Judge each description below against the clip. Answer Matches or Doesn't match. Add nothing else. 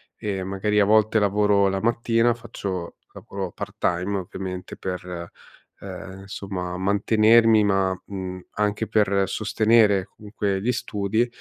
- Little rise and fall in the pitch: Matches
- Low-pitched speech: Matches